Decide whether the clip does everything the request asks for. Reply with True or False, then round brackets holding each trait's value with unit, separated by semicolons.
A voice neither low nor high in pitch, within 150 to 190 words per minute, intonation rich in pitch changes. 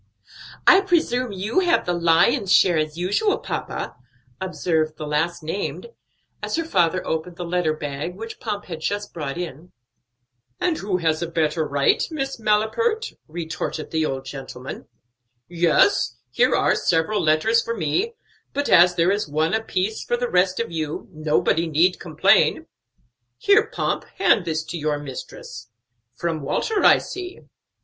True (175 Hz; 155 wpm; 5.9 semitones)